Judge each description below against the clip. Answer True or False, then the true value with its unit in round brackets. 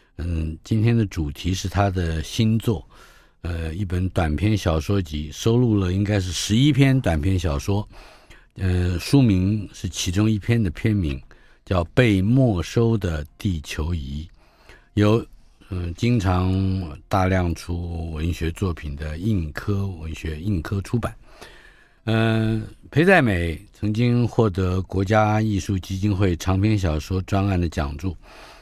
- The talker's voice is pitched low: True (95 Hz)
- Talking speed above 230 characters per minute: False (205 characters per minute)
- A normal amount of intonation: True (4.1 semitones)